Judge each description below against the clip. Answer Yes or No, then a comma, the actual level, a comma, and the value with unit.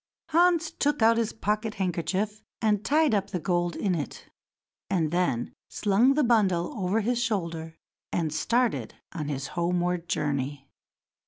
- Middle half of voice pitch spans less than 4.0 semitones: No, average, 5.0 semitones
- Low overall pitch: No, high, 195 Hz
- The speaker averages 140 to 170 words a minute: Yes, average, 145 wpm